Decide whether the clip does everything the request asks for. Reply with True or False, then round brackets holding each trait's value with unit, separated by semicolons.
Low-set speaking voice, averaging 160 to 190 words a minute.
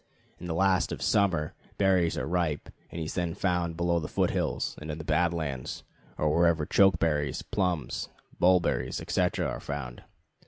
True (85 Hz; 170 wpm)